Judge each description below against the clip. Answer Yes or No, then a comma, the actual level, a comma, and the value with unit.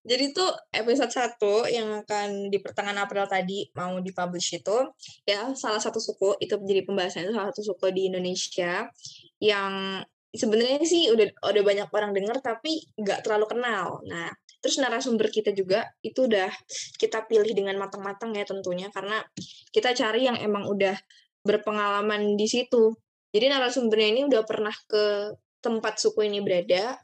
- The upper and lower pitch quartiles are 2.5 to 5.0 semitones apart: Yes, average, 2.9 semitones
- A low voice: No, high, 210 Hz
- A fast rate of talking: Yes, fast, 155 wpm